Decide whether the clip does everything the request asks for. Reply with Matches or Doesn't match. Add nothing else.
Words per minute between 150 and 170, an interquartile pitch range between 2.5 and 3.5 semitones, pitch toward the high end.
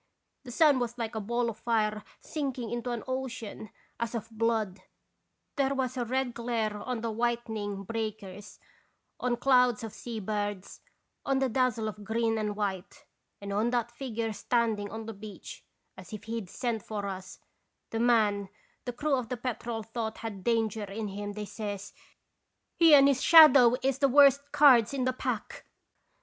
Doesn't match